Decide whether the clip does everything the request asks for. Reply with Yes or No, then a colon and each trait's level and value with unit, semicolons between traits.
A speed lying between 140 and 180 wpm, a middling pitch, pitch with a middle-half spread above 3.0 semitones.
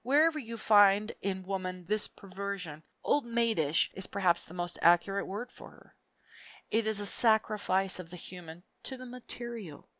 No: average, 160 wpm; high, 200 Hz; average, 4.1 semitones